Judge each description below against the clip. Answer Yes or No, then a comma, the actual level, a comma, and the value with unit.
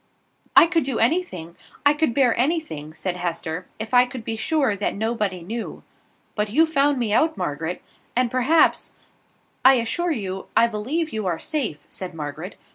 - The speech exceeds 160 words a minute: Yes, average, 175 wpm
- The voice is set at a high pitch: Yes, high, 230 Hz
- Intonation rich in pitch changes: Yes, wide, 7.5 semitones